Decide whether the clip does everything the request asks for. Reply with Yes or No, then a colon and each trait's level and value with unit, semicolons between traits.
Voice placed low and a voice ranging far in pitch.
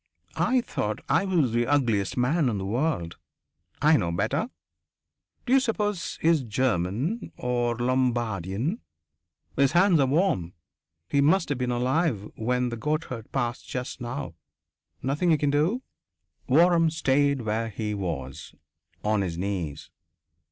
Yes: low, 125 Hz; wide, 6.5 semitones